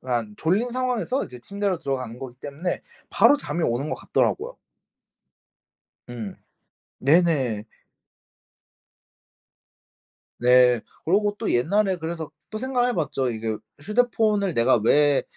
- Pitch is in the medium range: Yes, medium, 160 Hz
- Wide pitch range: Yes, wide, 9.0 semitones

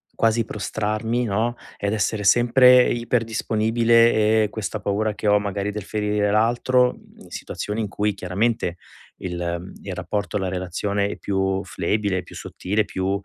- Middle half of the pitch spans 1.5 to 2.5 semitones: Yes, narrow, 2.2 semitones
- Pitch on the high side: No, low, 105 Hz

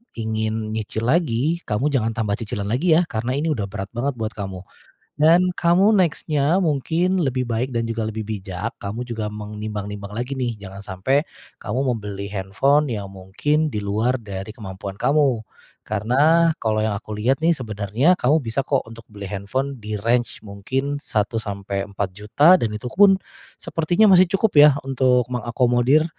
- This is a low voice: Yes, low, 115 Hz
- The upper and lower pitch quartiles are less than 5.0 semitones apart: No, wide, 5.5 semitones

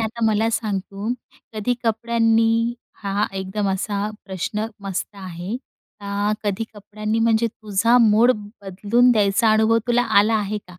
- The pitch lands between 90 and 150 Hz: No, high, 215 Hz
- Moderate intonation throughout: No, narrow, 2.1 semitones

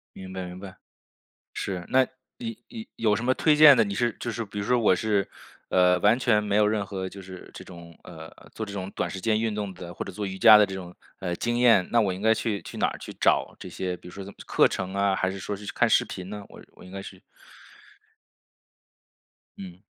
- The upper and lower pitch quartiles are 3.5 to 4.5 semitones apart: No, average, 2.9 semitones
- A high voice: No, low, 100 Hz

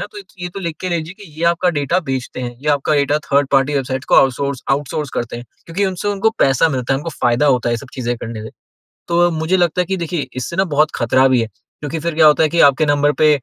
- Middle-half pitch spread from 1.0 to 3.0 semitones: No, average, 4.5 semitones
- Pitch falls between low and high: Yes, medium, 145 Hz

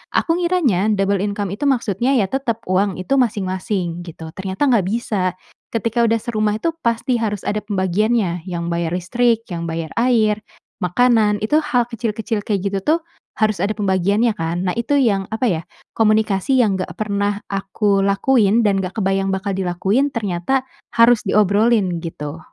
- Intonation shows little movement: No, average, 3.6 semitones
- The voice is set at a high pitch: Yes, high, 205 Hz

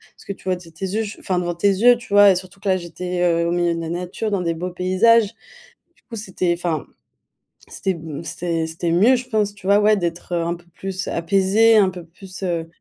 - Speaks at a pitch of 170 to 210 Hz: Yes, medium, 185 Hz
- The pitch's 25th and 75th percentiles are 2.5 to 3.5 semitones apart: Yes, average, 2.8 semitones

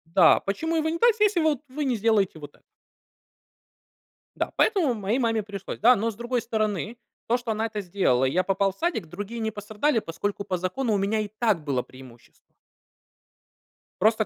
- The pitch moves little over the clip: No, average, 3.8 semitones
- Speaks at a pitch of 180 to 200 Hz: No, high, 215 Hz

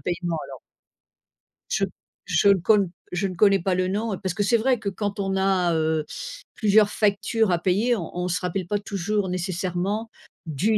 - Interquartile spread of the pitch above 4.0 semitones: No, average, 2.7 semitones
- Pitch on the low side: No, high, 195 Hz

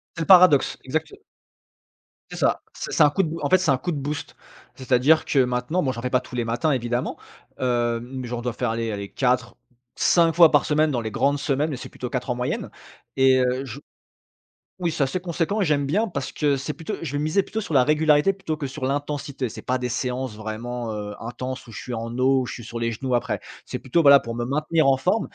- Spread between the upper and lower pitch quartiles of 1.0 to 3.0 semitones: No, average, 3.8 semitones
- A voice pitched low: Yes, low, 130 Hz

